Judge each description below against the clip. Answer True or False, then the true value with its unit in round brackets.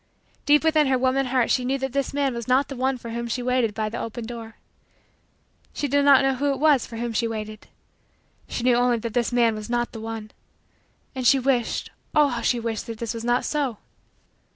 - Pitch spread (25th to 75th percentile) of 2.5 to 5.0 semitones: True (2.8 semitones)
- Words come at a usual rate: False (225 wpm)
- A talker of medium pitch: False (245 Hz)